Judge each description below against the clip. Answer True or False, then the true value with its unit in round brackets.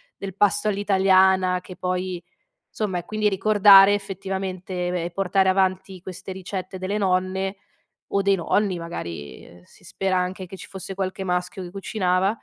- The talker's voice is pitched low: False (190 Hz)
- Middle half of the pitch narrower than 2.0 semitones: True (1.3 semitones)